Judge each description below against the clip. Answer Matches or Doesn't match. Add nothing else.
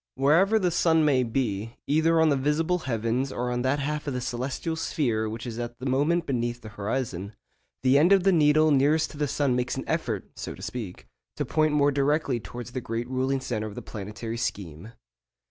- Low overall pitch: Matches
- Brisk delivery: Matches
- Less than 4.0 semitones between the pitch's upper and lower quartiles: Doesn't match